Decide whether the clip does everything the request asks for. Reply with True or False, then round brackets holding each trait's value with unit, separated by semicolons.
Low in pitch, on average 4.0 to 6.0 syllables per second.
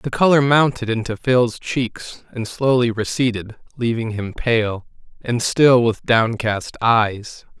False (120 Hz; 3.7 syllables/s)